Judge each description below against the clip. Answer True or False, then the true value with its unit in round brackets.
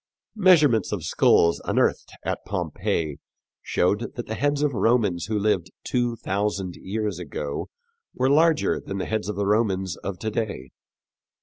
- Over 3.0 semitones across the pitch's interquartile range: True (4.0 semitones)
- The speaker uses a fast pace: False (160 wpm)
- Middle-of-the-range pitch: False (105 Hz)